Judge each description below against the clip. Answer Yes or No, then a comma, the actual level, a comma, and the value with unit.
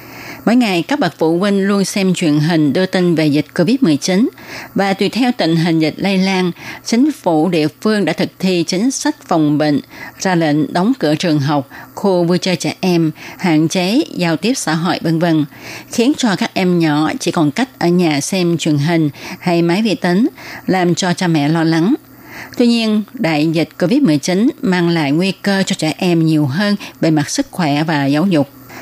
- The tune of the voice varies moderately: Yes, average, 4.0 semitones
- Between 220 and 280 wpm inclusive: No, average, 200 wpm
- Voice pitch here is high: No, medium, 175 Hz